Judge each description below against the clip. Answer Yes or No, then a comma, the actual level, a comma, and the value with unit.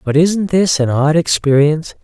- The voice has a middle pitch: Yes, medium, 155 Hz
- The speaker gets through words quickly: No, average, 175 wpm